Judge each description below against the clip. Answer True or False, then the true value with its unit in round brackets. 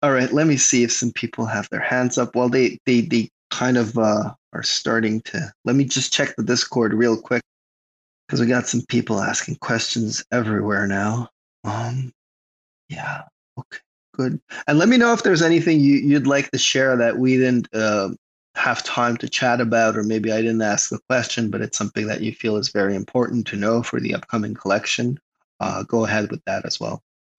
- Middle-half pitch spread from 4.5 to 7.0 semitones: False (2.6 semitones)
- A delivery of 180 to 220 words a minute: True (205 wpm)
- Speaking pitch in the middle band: False (120 Hz)